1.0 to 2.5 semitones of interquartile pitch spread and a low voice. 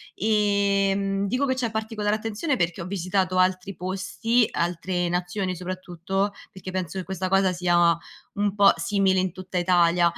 No: narrow, 2.2 semitones; high, 190 Hz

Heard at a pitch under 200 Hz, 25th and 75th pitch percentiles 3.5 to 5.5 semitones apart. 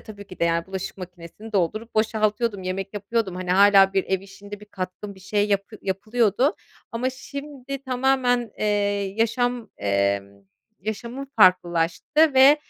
No: high, 205 Hz; average, 4.5 semitones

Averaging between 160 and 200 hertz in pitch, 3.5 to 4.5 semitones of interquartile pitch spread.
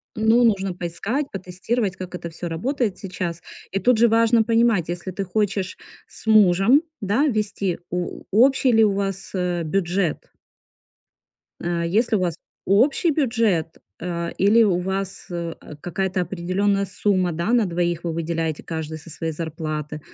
Yes: high, 190 Hz; average, 4.1 semitones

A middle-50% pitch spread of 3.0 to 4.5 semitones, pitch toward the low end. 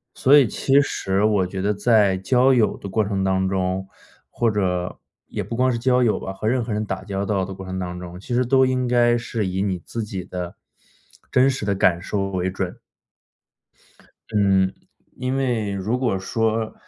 Yes: average, 4.1 semitones; low, 100 Hz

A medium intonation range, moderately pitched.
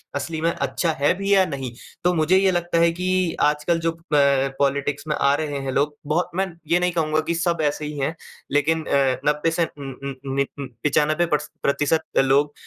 Yes: average, 3.1 semitones; medium, 150 Hz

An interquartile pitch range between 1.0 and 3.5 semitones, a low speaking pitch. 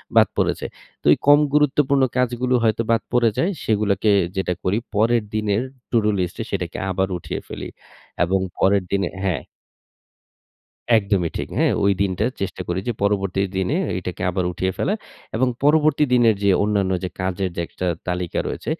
No: average, 4.2 semitones; low, 100 Hz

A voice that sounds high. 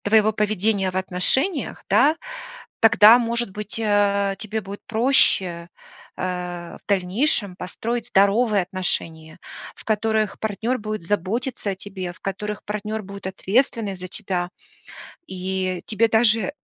Yes: high, 205 Hz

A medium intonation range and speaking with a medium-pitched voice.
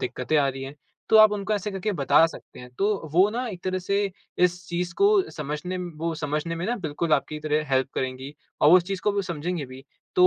Yes: average, 4.7 semitones; medium, 170 Hz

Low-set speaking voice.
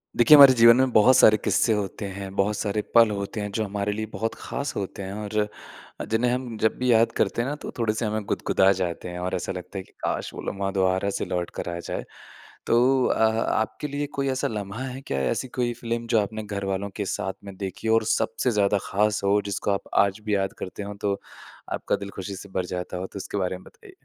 Yes: low, 105 Hz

